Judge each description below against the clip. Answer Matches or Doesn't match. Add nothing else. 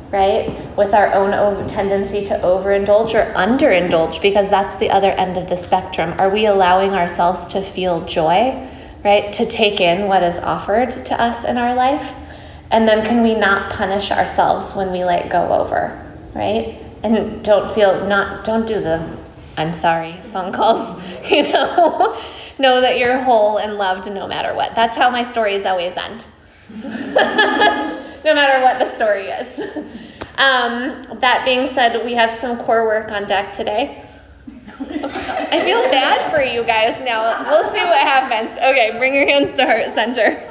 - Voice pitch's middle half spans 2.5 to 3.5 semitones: Doesn't match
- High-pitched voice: Matches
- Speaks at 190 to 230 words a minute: Doesn't match